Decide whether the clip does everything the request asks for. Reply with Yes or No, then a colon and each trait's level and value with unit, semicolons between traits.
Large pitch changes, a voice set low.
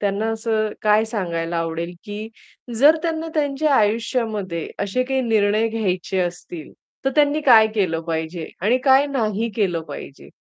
No: wide, 5.9 semitones; high, 215 Hz